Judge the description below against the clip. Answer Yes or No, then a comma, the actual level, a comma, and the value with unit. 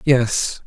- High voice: No, low, 120 Hz